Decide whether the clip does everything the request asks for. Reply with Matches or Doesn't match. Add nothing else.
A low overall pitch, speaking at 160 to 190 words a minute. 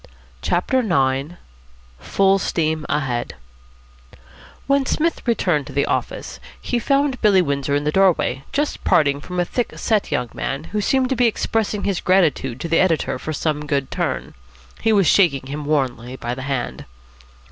Doesn't match